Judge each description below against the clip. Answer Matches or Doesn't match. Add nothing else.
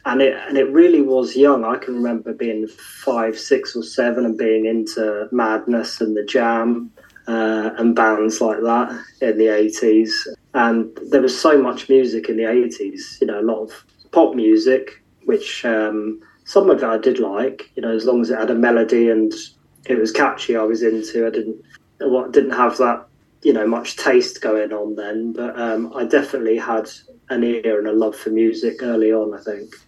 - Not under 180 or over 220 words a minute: Matches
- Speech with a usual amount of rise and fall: Doesn't match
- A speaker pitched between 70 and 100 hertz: Doesn't match